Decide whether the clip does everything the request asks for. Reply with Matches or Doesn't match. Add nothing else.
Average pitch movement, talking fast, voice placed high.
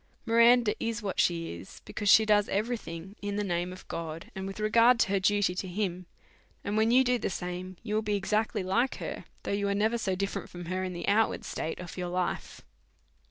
Matches